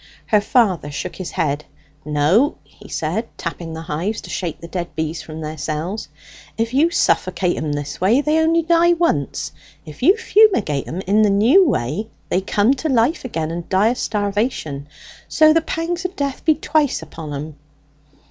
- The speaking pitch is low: No, high, 200 Hz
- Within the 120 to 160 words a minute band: No, average, 180 wpm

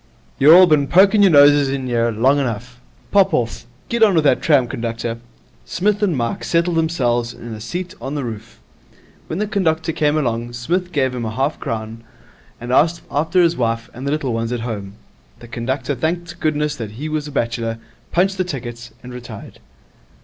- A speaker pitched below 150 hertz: Yes, low, 135 Hz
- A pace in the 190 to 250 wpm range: Yes, average, 195 wpm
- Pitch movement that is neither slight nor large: No, wide, 5.7 semitones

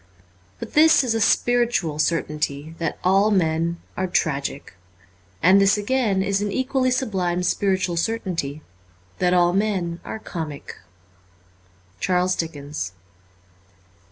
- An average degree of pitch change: Yes, average, 4.1 semitones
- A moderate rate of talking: No, slow, 115 wpm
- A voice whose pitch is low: No, medium, 180 Hz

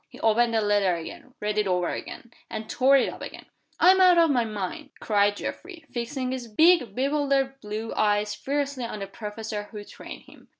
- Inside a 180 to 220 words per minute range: Yes, average, 195 wpm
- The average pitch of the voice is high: Yes, high, 230 Hz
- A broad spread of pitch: No, average, 4.7 semitones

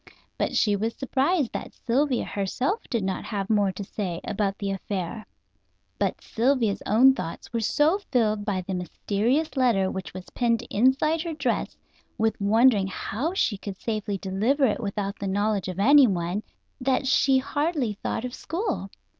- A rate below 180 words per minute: Yes, average, 165 wpm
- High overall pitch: Yes, high, 220 Hz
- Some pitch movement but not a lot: Yes, average, 4.9 semitones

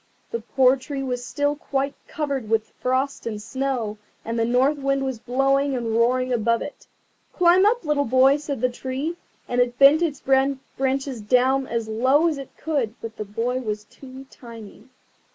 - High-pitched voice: Yes, very high, 260 Hz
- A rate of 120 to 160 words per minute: No, average, 175 wpm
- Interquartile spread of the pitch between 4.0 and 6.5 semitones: No, average, 2.8 semitones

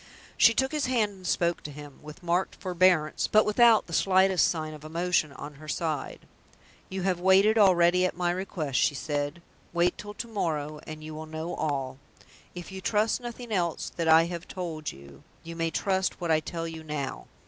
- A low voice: No, medium, 170 Hz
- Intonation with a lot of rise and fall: No, average, 3.5 semitones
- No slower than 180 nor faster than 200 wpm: Yes, average, 195 wpm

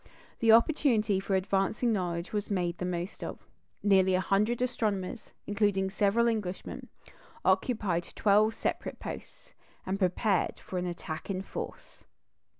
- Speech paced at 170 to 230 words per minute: No, slow, 135 wpm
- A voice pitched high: Yes, high, 195 Hz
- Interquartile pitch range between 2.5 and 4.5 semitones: Yes, average, 2.8 semitones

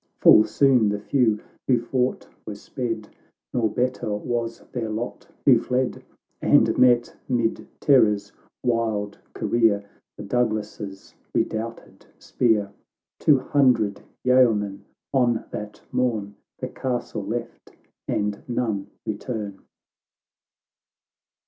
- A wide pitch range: No, average, 3.0 semitones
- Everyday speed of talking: No, slow, 105 wpm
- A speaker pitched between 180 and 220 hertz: No, low, 115 Hz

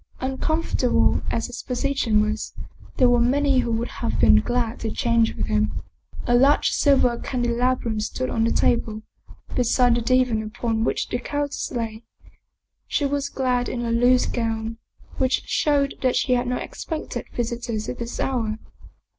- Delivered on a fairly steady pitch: Yes, narrow, 2.1 semitones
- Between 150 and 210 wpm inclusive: Yes, average, 160 wpm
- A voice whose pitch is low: No, high, 245 Hz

